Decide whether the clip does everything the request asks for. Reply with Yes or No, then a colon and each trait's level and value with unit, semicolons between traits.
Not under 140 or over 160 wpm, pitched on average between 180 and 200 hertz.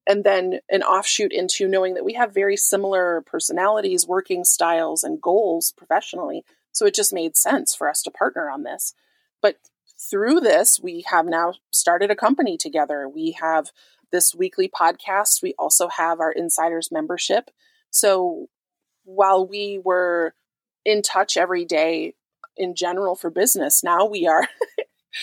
Yes: average, 150 wpm; high, 190 Hz